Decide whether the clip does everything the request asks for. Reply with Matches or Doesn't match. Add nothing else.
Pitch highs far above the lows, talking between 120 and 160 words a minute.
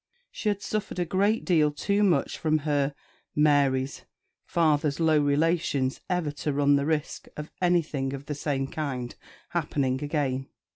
Doesn't match